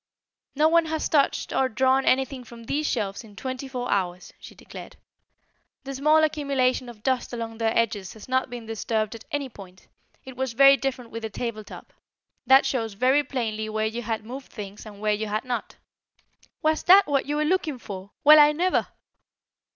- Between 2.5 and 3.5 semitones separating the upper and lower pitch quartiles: No, average, 4.2 semitones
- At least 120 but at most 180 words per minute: No, average, 190 wpm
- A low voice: No, very high, 250 Hz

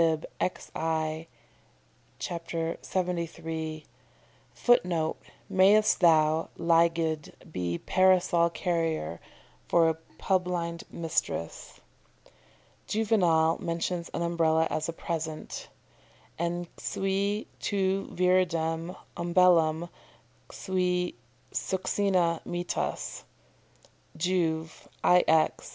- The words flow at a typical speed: No, slow, 70 wpm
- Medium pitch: Yes, medium, 170 Hz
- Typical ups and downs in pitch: No, narrow, 2.1 semitones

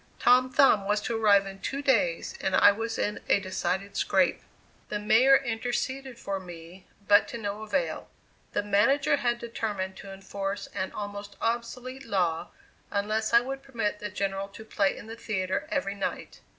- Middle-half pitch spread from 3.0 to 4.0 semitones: Yes, average, 3.3 semitones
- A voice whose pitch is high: Yes, high, 210 Hz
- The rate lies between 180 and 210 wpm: No, average, 170 wpm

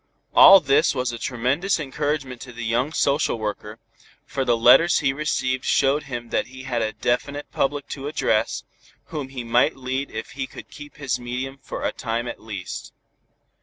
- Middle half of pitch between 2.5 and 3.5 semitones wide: Yes, average, 2.9 semitones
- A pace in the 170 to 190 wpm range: Yes, average, 180 wpm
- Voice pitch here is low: Yes, low, 130 Hz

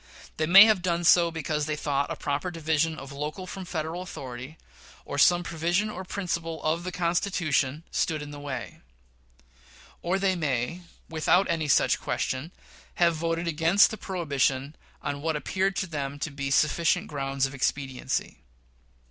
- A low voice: No, medium, 160 Hz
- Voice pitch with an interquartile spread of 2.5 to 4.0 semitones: Yes, average, 3.6 semitones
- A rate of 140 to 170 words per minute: Yes, average, 160 wpm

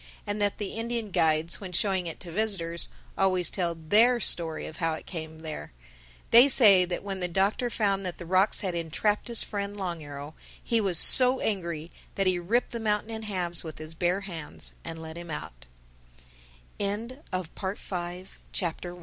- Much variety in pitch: No, average, 3.8 semitones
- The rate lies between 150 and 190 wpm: Yes, average, 160 wpm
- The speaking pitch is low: No, medium, 185 Hz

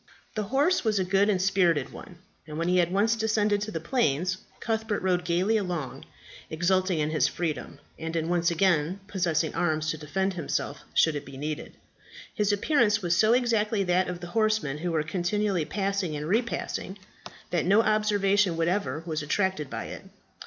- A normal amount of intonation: Yes, average, 4.2 semitones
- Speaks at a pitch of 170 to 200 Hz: Yes, medium, 185 Hz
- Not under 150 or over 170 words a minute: No, average, 180 wpm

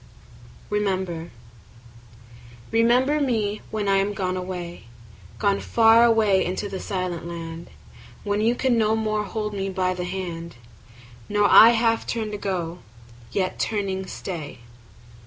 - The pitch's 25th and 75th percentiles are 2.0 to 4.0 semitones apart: Yes, average, 3.1 semitones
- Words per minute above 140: No, slow, 135 wpm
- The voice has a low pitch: No, high, 200 Hz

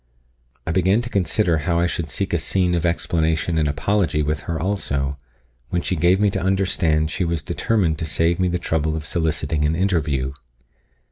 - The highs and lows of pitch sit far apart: No, average, 3.1 semitones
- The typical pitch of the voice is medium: No, very low, 85 Hz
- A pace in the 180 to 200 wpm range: Yes, average, 190 wpm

